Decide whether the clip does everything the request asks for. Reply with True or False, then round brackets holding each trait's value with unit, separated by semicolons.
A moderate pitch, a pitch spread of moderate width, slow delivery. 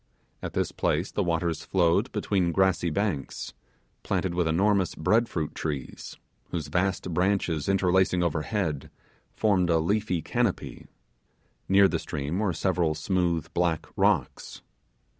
False (90 Hz; 3.0 semitones; 125 wpm)